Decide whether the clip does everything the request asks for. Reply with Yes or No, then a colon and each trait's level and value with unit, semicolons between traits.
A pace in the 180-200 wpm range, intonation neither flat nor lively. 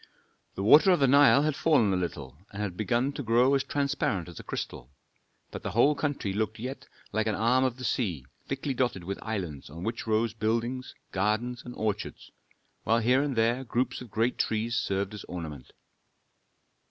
Yes: average, 190 wpm; average, 4.3 semitones